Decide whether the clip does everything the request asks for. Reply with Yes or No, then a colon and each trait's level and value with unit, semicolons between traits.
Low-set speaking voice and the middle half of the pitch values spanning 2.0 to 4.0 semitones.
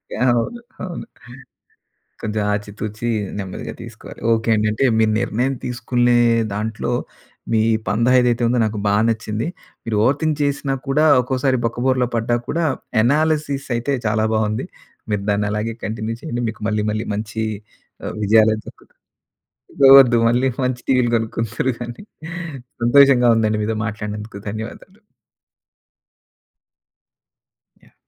Yes: low, 115 Hz; average, 2.9 semitones